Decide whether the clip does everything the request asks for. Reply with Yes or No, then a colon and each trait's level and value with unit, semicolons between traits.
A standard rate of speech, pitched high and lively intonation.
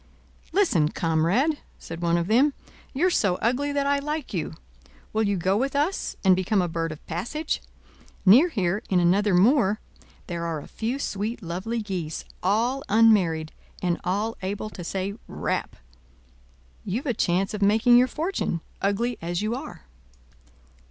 Yes: average, 160 wpm; high, 205 Hz; wide, 5.8 semitones